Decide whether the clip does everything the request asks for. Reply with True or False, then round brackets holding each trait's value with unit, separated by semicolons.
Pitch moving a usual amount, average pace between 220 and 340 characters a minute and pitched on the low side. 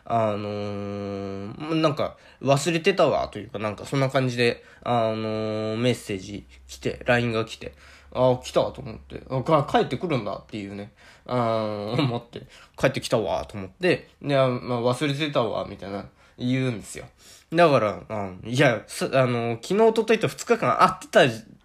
True (4.9 semitones; 315 characters per minute; 120 Hz)